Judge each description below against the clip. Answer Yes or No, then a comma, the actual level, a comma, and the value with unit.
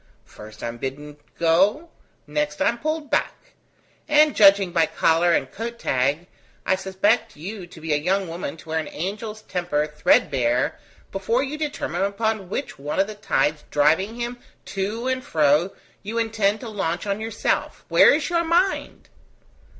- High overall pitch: Yes, high, 195 Hz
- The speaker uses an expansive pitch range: Yes, wide, 6.3 semitones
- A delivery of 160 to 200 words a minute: Yes, average, 165 wpm